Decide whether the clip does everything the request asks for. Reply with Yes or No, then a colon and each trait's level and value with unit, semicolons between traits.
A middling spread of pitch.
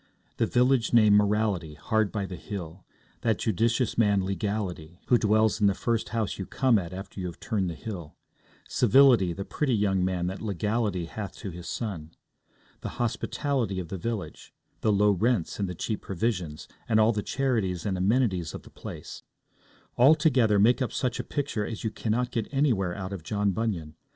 Yes: average, 3.8 semitones